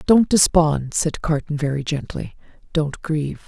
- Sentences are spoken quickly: No, average, 140 wpm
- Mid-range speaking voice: Yes, medium, 155 Hz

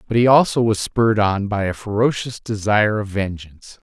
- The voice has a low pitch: Yes, low, 105 Hz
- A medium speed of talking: Yes, average, 185 wpm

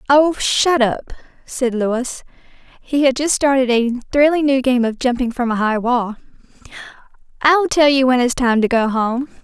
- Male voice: No, female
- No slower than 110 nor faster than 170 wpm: No, average, 180 wpm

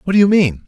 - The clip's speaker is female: No, male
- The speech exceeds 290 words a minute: Yes, fast, 355 wpm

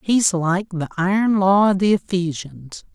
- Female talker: Yes, female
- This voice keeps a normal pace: Yes, average, 165 wpm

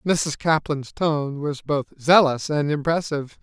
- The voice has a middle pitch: Yes, medium, 150 Hz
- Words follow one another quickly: No, average, 140 wpm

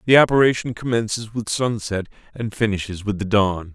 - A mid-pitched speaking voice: No, low, 110 Hz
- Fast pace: No, average, 160 wpm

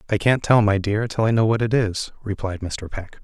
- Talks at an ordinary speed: No, fast, 260 wpm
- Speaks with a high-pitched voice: No, low, 105 Hz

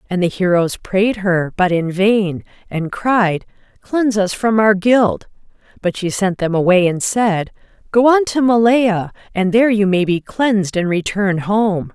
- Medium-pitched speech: No, high, 200 Hz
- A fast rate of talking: No, average, 175 wpm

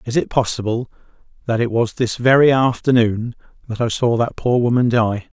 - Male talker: Yes, male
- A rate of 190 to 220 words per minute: No, average, 180 wpm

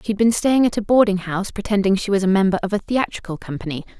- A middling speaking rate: No, fast, 240 wpm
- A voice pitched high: Yes, high, 200 Hz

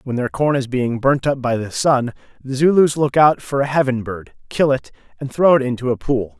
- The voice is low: Yes, low, 130 Hz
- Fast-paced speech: Yes, fast, 245 wpm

